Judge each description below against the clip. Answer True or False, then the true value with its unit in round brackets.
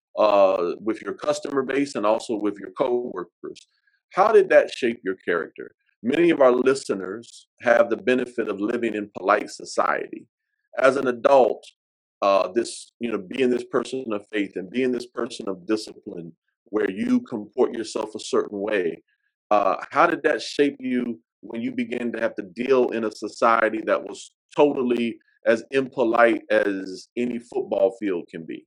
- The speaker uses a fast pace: False (165 wpm)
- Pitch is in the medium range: False (125 Hz)